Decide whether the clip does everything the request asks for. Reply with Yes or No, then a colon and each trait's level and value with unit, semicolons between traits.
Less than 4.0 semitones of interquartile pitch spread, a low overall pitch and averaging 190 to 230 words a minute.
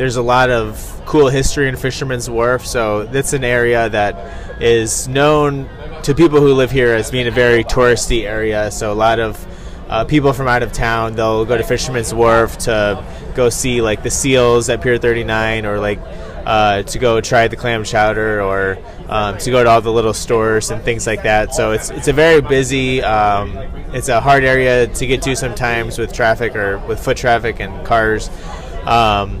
Yes: average, 3.0 semitones; low, 115 Hz; average, 200 wpm